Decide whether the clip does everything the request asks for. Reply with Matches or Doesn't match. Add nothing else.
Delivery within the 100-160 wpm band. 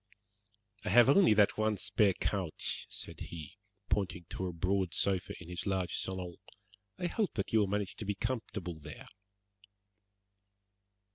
Matches